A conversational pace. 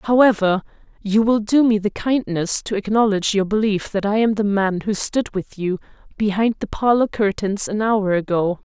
Yes: average, 185 wpm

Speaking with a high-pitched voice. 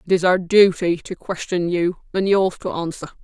No: medium, 180 Hz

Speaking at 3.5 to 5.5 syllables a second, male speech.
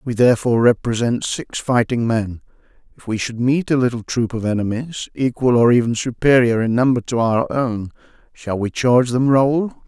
Yes: 5.1 syllables/s; male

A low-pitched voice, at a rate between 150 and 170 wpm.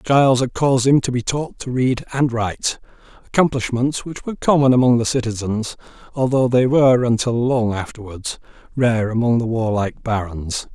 Yes: low, 120 Hz; average, 160 wpm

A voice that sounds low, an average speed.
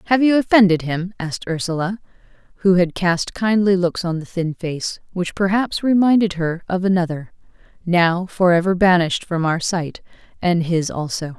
No: medium, 180 Hz; average, 160 wpm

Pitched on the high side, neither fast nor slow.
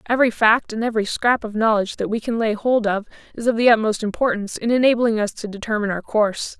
No: high, 220 Hz; fast, 225 wpm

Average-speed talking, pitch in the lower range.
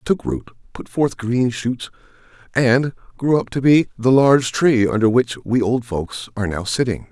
Yes: average, 195 wpm; low, 120 Hz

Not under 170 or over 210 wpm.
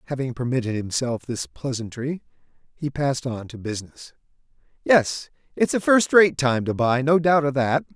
No: average, 160 wpm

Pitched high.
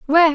Yes: very high, 315 Hz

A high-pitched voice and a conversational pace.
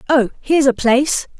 Yes: very high, 265 Hz; average, 170 wpm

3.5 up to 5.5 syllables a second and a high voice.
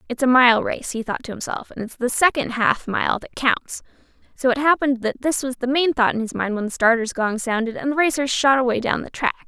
No: 5.7 syllables/s; very high, 250 Hz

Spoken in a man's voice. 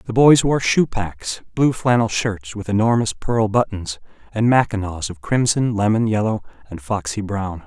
Yes: male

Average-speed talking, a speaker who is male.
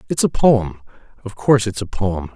Yes: average, 180 wpm; male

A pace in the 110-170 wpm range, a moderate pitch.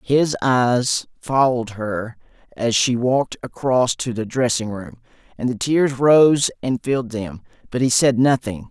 No: average, 160 wpm; low, 125 Hz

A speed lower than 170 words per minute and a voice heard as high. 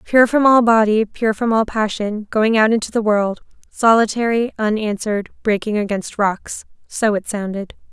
Yes: average, 150 wpm; high, 215 Hz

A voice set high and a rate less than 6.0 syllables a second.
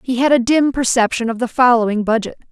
No: high, 245 Hz; 6.1 syllables/s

